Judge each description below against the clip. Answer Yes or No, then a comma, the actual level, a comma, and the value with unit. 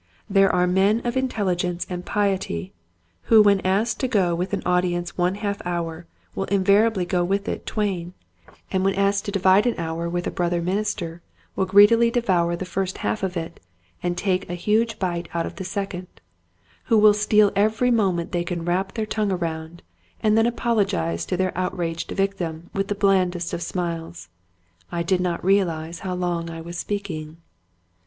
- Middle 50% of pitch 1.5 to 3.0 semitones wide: Yes, average, 2.7 semitones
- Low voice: No, medium, 185 Hz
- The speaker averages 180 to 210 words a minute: Yes, average, 190 wpm